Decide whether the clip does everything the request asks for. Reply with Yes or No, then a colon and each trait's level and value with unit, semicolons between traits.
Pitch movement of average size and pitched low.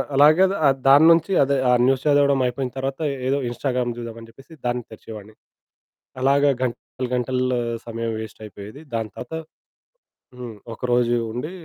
Yes: average, 3.2 semitones; low, 125 Hz